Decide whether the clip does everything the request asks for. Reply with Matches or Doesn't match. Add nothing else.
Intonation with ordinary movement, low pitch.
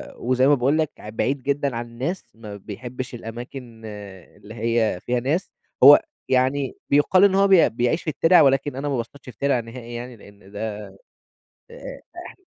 Matches